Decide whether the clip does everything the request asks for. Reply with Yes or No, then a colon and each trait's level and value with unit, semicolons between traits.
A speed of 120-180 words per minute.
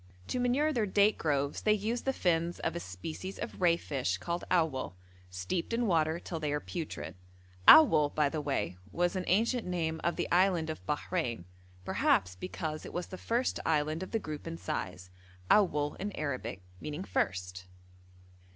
Yes: average, 175 wpm